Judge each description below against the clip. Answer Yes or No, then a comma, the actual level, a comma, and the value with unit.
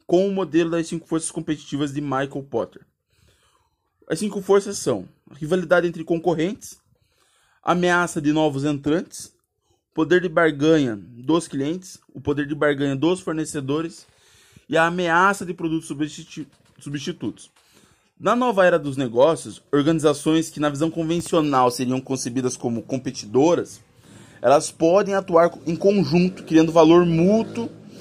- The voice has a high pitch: No, medium, 160 Hz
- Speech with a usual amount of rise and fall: Yes, average, 3.1 semitones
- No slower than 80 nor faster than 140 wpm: Yes, average, 135 wpm